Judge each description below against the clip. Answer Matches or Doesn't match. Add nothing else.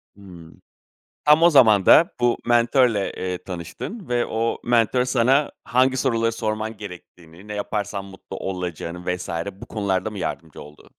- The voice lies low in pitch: Matches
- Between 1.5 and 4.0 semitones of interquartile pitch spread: Doesn't match